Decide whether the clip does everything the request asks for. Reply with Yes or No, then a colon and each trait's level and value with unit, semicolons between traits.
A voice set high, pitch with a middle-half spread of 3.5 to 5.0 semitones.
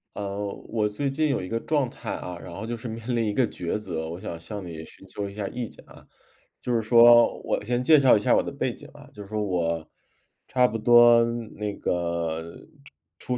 No: low, 105 Hz; average, 4.6 semitones